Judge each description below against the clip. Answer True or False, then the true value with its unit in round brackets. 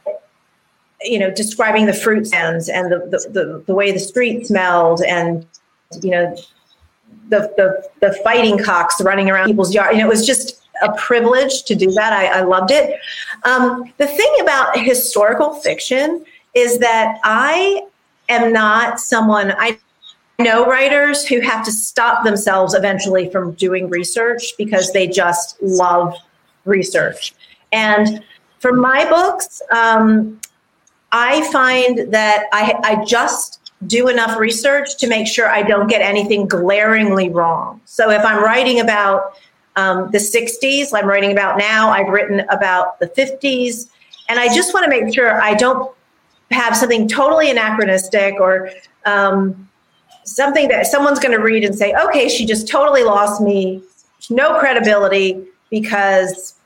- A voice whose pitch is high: True (220 Hz)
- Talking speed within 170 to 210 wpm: False (150 wpm)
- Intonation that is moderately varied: True (4.3 semitones)